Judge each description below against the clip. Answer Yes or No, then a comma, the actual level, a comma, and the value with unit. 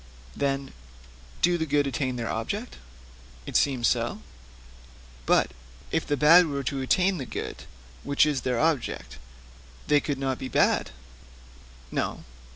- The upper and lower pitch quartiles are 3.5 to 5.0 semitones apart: No, average, 3.0 semitones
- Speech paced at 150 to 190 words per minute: No, average, 140 wpm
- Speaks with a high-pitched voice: No, medium, 140 Hz